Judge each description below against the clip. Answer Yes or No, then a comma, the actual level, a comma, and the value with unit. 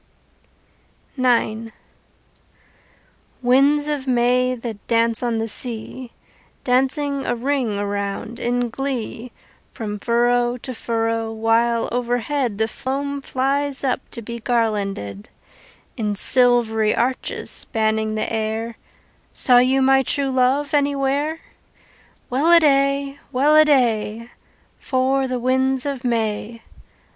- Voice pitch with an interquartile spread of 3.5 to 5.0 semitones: No, average, 3.1 semitones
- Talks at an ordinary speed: No, slow, 105 wpm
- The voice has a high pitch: Yes, high, 245 Hz